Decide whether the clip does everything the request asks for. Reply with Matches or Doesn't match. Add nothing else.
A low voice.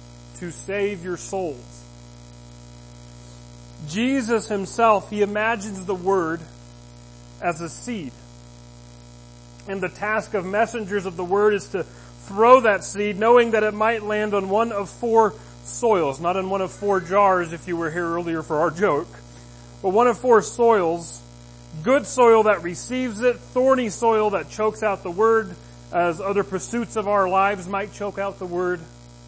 Doesn't match